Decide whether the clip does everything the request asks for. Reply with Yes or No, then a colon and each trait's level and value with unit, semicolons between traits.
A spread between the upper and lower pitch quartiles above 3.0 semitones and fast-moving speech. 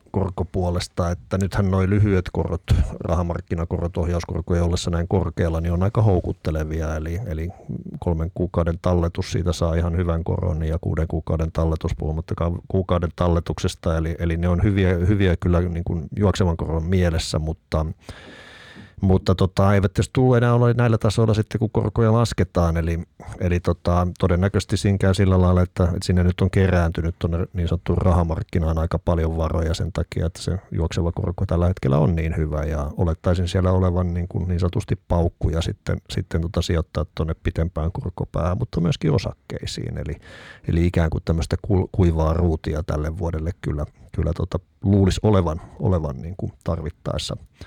No: narrow, 2.5 semitones; fast, 160 wpm